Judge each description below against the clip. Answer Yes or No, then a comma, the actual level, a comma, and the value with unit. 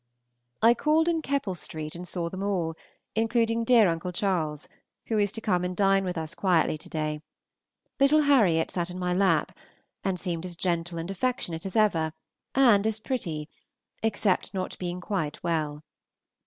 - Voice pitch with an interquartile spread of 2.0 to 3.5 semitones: No, average, 4.7 semitones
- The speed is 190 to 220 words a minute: No, average, 170 wpm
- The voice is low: No, medium, 185 Hz